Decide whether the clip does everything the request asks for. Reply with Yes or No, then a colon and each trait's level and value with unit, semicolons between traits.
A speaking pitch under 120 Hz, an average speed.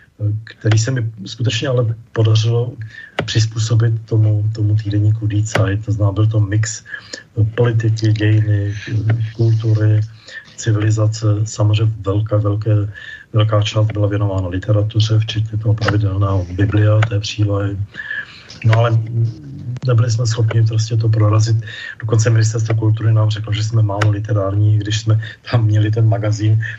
Yes: low, 110 Hz; average, 130 wpm